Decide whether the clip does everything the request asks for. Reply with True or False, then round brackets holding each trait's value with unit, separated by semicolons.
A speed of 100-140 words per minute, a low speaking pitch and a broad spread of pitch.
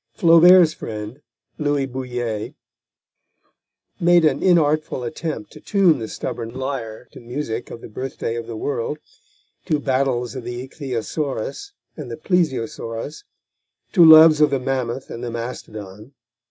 False (135 wpm; 130 Hz; 4.7 semitones)